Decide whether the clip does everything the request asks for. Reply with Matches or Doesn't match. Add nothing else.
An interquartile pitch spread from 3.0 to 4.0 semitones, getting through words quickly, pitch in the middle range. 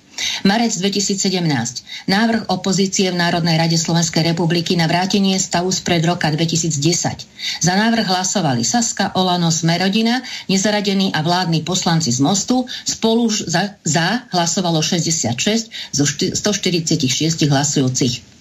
Doesn't match